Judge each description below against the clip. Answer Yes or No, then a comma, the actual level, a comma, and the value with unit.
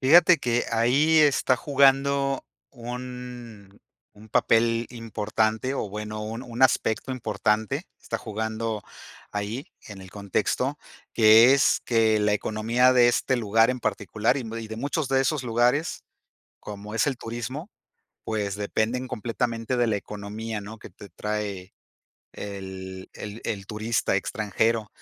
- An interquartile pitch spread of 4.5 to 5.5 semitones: No, average, 3.0 semitones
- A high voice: No, low, 115 Hz